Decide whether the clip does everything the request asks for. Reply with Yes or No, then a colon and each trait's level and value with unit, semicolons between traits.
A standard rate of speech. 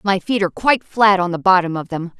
No: fast, 275 wpm